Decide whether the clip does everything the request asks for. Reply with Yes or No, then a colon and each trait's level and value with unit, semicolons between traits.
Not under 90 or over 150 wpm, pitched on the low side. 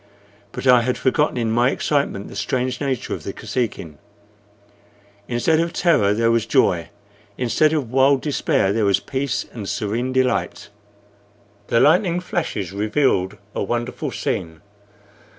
Yes: average, 140 wpm; low, 125 Hz